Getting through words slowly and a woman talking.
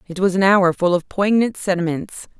No: average, 200 wpm; female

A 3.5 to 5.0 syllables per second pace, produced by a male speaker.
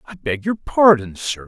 Yes: 4.2 syllables/s; male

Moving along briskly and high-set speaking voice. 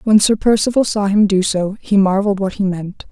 Yes: fast, 230 wpm; high, 200 Hz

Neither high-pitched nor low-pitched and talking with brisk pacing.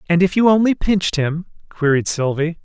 No: medium, 170 Hz; average, 180 wpm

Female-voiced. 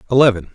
No: male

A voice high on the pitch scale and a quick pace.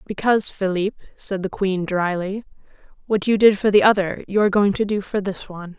Yes: high, 195 Hz; fast, 210 wpm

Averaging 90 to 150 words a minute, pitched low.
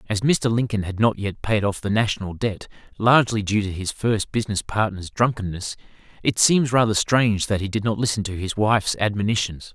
No: average, 195 wpm; low, 105 Hz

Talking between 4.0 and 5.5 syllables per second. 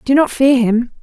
Yes: 4.7 syllables/s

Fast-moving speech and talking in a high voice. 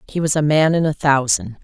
No: fast, 255 wpm; medium, 145 Hz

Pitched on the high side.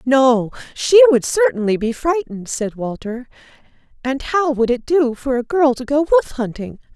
Yes: very high, 265 Hz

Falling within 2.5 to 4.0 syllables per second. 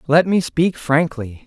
Yes: 3.8 syllables/s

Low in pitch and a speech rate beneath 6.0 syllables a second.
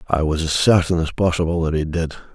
No: very low, 80 Hz; 6.1 syllables/s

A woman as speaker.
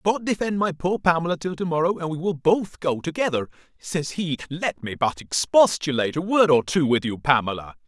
No: male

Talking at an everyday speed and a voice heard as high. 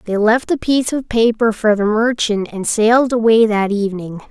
Yes: average, 195 wpm; high, 220 Hz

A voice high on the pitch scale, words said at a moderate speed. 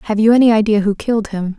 No: high, 215 Hz; fast, 265 wpm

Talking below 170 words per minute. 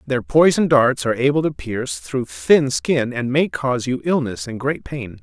No: fast, 205 wpm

